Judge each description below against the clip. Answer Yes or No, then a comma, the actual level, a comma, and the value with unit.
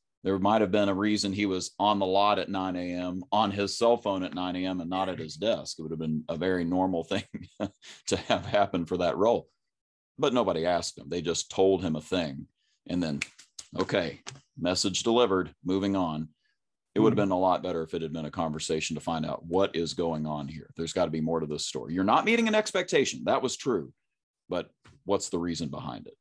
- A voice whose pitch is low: Yes, very low, 95 Hz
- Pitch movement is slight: No, average, 3.3 semitones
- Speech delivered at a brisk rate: Yes, fast, 230 wpm